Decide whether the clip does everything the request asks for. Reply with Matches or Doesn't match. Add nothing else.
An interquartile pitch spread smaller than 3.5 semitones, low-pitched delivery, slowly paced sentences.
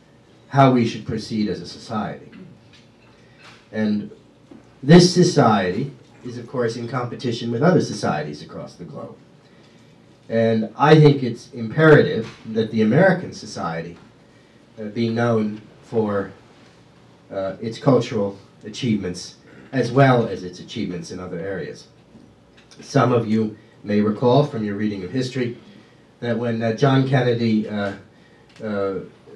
Matches